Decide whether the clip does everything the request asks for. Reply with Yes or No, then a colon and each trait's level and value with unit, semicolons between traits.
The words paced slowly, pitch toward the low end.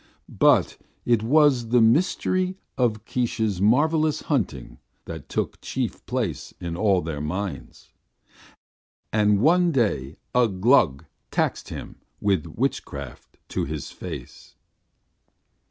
Yes: slow, 110 wpm; low, 110 Hz